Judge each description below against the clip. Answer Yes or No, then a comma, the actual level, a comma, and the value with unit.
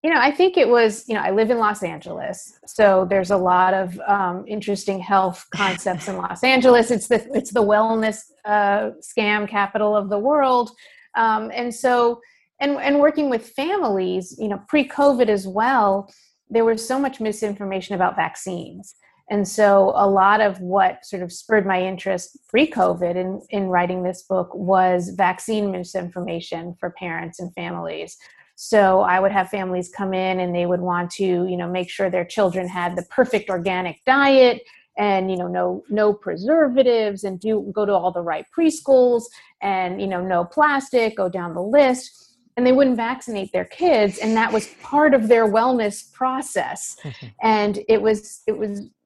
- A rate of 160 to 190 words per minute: Yes, average, 180 wpm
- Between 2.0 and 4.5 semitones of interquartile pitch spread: Yes, average, 4.2 semitones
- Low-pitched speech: No, high, 205 Hz